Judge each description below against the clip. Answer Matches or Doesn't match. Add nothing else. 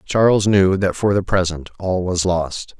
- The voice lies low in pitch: Matches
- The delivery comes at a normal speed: Matches